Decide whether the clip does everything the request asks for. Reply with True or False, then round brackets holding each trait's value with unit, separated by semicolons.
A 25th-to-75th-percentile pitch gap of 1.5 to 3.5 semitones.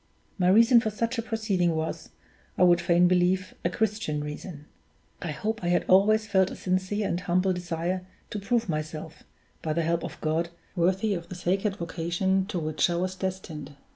True (2.7 semitones)